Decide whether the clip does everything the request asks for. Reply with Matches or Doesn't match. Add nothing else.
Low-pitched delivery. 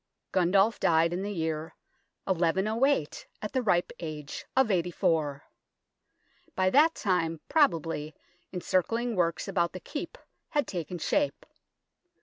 Doesn't match